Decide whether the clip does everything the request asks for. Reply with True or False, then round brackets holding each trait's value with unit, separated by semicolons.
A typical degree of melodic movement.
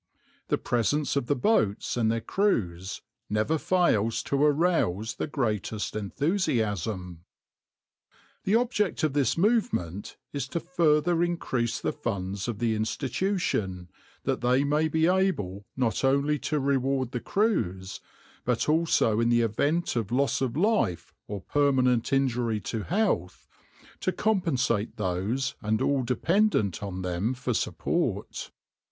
False (6.9 semitones)